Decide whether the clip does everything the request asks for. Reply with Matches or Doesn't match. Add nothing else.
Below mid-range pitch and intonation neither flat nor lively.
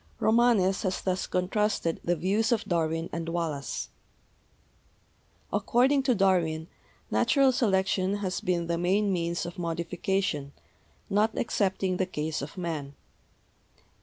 Doesn't match